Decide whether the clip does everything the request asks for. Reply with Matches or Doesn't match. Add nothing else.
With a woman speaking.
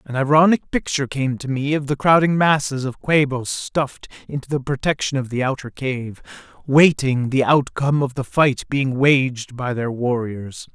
Doesn't match